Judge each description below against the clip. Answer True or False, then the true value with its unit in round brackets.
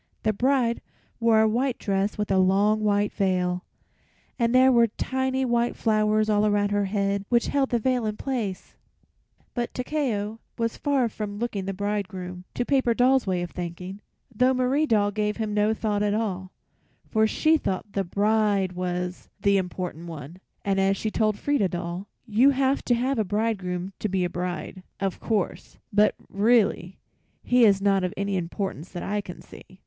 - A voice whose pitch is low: False (210 Hz)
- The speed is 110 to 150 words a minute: False (180 wpm)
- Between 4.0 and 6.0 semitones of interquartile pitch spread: False (3.5 semitones)